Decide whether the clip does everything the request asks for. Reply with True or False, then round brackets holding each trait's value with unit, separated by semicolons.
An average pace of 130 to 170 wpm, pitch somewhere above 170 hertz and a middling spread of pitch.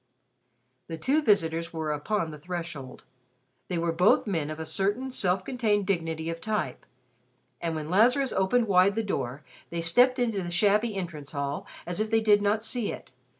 False (180 wpm; 185 Hz; 4.8 semitones)